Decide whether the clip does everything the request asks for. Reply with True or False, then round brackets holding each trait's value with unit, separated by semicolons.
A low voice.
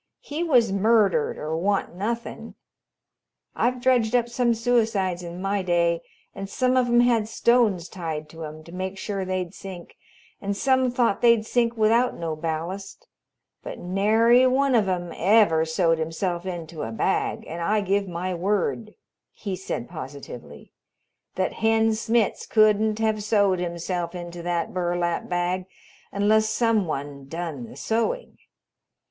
False (195 Hz)